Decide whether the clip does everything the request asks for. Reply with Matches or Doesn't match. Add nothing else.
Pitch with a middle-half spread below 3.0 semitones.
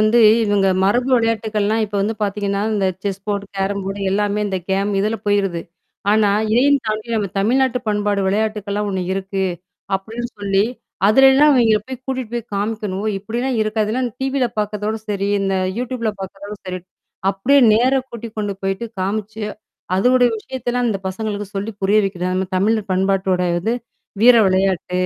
Matches